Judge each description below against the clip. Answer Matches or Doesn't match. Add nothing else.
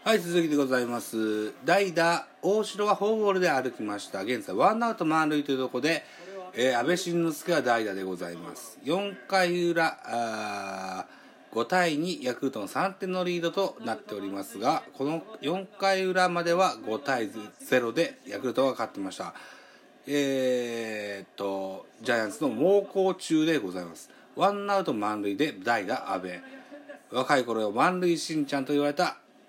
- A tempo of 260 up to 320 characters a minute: Matches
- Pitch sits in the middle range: Matches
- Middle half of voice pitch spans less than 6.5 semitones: Doesn't match